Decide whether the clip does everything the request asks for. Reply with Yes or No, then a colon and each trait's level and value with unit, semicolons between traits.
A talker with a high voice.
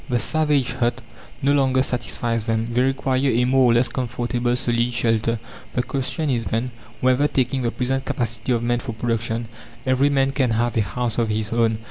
No: low, 120 Hz